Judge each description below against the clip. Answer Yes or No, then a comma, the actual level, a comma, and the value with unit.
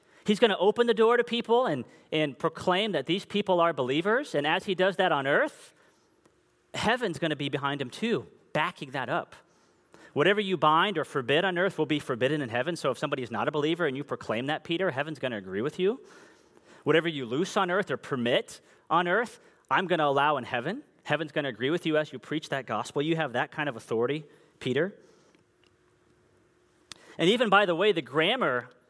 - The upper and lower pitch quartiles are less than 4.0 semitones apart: No, average, 4.9 semitones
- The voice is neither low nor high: Yes, medium, 165 Hz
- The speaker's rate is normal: No, fast, 215 wpm